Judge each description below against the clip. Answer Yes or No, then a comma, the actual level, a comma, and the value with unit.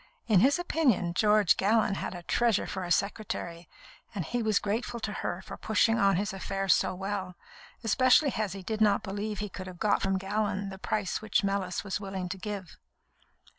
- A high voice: Yes, high, 200 Hz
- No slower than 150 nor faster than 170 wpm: No, average, 195 wpm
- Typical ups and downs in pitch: No, narrow, 2.3 semitones